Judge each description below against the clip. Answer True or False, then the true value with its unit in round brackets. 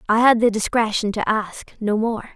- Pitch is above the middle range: True (220 Hz)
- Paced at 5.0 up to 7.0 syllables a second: False (4.7 syllables/s)